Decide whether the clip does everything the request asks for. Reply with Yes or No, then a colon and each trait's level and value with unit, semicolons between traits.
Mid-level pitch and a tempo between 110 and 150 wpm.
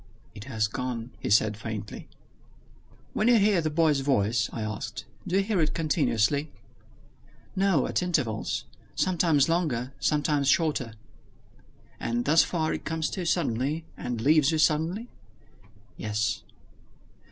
Yes: medium, 145 Hz; slow, 135 wpm